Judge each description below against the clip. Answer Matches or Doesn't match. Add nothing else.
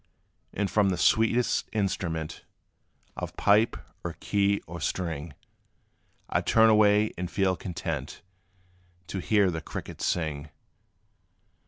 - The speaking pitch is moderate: Doesn't match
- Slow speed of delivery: Matches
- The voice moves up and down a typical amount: Matches